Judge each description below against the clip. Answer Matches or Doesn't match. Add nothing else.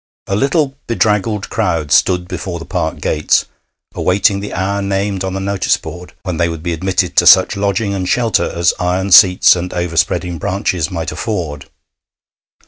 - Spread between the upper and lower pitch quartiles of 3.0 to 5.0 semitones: Doesn't match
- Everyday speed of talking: Matches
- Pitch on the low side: Matches